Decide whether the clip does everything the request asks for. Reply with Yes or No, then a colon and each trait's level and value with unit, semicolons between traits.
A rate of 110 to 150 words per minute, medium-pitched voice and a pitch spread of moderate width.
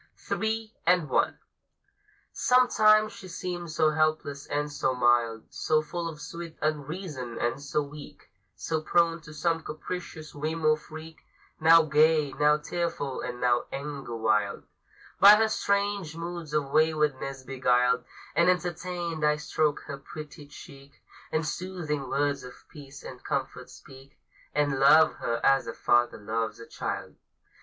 Yes: average, 145 wpm; medium, 150 Hz; average, 3.5 semitones